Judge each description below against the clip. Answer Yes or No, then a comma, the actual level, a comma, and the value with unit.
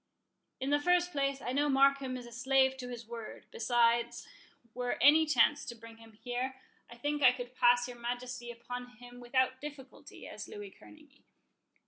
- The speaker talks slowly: No, average, 175 wpm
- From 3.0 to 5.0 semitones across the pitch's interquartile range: No, narrow, 2.4 semitones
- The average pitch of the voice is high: Yes, very high, 250 Hz